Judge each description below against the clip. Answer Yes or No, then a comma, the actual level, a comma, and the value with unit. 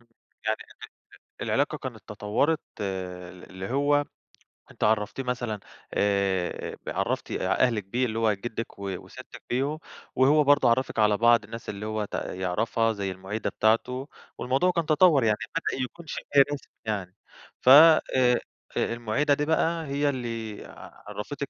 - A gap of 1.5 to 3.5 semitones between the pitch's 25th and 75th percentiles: No, average, 5.1 semitones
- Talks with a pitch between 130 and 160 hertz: No, low, 115 Hz